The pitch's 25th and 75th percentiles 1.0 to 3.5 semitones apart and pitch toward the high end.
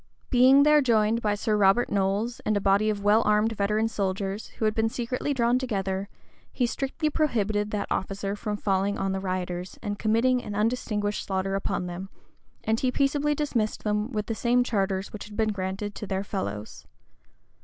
Yes: average, 3.1 semitones; high, 210 Hz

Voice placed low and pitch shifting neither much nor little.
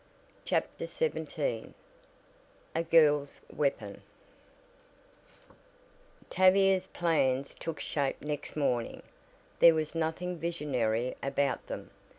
No: medium, 155 Hz; average, 3.7 semitones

